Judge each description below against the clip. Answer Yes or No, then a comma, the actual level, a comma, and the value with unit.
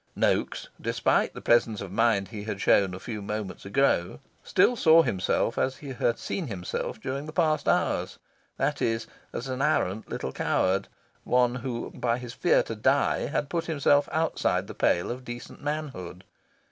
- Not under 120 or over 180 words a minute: Yes, average, 170 wpm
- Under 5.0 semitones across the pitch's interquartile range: No, wide, 5.6 semitones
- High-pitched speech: No, low, 120 Hz